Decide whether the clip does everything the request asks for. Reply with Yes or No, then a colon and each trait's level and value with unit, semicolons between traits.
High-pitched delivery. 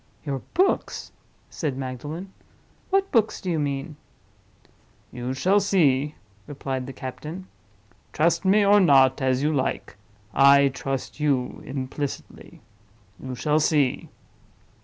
No: medium, 140 Hz